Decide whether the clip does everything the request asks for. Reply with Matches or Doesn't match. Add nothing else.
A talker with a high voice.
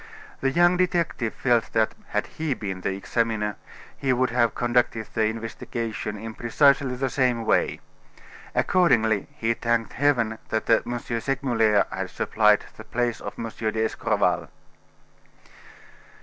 Doesn't match